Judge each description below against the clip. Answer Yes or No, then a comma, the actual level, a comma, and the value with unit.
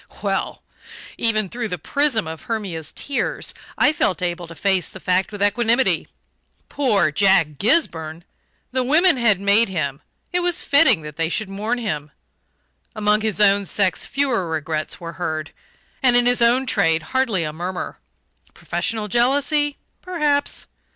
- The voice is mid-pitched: No, high, 205 Hz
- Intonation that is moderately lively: No, wide, 6.4 semitones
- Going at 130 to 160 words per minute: Yes, average, 150 wpm